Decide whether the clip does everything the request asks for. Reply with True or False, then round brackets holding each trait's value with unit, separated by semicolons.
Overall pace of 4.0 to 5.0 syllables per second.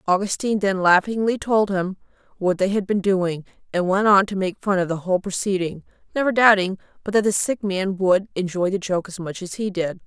False (5.5 syllables/s)